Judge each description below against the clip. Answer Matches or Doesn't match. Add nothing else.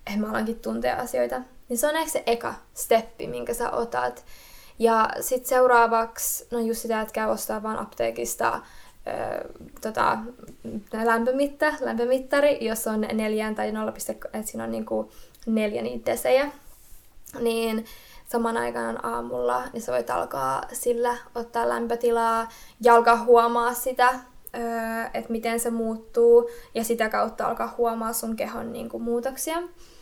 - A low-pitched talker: Doesn't match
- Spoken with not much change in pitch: Matches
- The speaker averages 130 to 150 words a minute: Matches